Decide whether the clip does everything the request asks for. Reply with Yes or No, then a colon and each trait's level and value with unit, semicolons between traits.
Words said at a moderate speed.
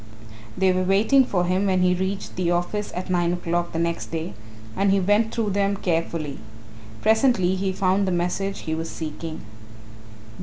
Yes: average, 175 wpm